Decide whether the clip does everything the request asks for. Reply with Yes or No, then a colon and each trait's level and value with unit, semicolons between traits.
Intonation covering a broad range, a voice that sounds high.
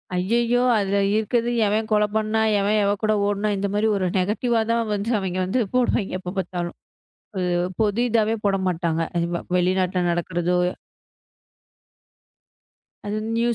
No: average, 3.0 semitones; high, 200 Hz